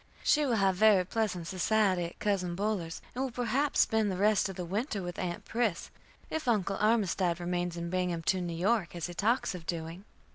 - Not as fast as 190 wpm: No, average, 195 wpm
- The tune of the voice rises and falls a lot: No, average, 3.8 semitones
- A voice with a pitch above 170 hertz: Yes, high, 190 Hz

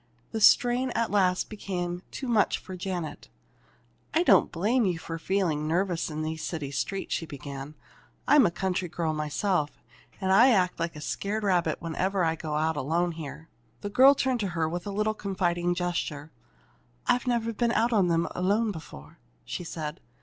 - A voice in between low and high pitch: Yes, medium, 180 Hz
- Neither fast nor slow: Yes, average, 180 wpm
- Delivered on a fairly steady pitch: No, average, 4.4 semitones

